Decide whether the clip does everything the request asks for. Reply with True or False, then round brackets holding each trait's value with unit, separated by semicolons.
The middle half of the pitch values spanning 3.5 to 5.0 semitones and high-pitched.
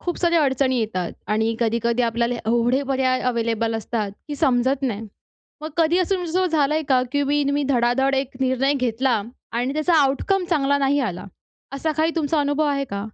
True (3.8 semitones; 265 Hz)